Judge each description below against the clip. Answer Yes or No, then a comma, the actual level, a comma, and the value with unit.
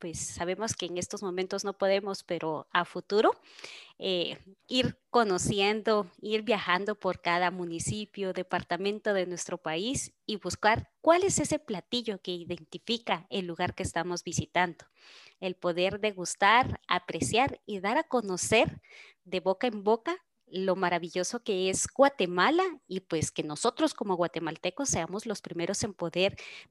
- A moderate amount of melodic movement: Yes, average, 3.3 semitones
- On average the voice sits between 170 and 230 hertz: Yes, medium, 185 Hz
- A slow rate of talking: No, average, 145 wpm